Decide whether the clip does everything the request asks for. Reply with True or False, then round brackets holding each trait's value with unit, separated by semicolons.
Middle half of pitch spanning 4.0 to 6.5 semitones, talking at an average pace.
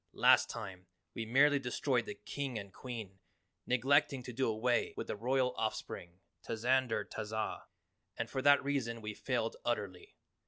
False (3.3 semitones; 155 wpm)